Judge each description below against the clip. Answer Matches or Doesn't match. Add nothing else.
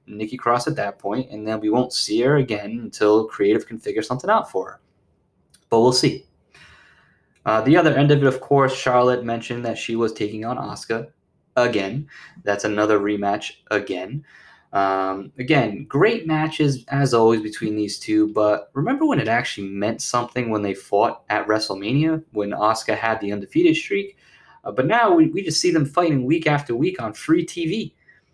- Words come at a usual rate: Matches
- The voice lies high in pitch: Doesn't match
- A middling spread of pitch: Doesn't match